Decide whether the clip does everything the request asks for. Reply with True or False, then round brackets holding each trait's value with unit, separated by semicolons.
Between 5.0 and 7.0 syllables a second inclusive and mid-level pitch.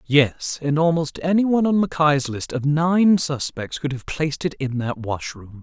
False (4.6 syllables/s; 150 Hz)